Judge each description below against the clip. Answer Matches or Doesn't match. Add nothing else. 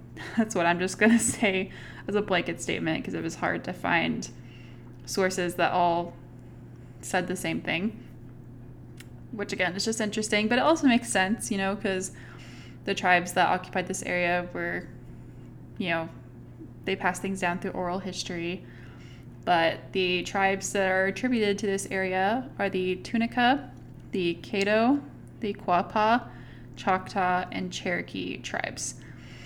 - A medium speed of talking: Matches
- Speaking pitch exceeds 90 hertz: Matches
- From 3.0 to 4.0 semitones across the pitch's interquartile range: Matches